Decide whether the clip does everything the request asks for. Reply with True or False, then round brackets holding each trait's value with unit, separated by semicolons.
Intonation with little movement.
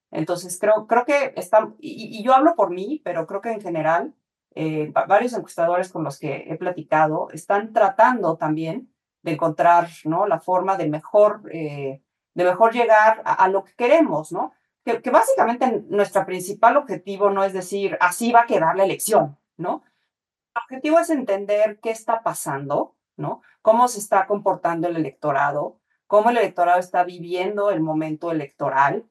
False (5.1 semitones)